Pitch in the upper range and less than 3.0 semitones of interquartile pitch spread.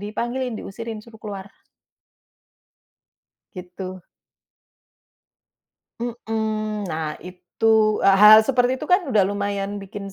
Yes: high, 210 Hz; narrow, 2.4 semitones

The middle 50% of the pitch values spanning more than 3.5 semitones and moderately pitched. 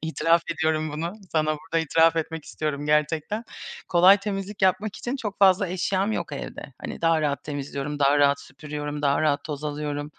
Yes: average, 3.9 semitones; medium, 155 Hz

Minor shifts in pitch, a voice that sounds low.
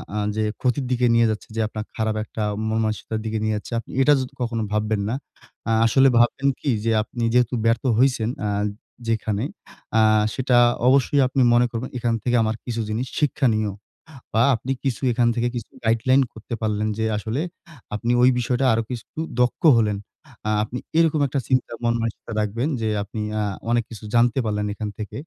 Yes: narrow, 2.3 semitones; low, 115 Hz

